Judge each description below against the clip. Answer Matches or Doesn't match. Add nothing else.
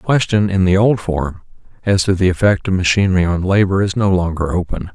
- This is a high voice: Doesn't match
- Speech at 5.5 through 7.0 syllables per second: Matches